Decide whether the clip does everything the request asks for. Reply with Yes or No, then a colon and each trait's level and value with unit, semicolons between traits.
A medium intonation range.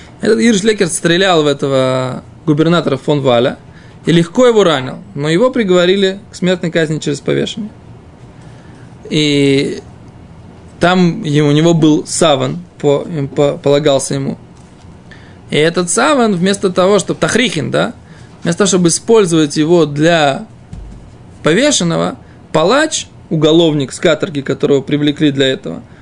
Yes: average, 4.5 semitones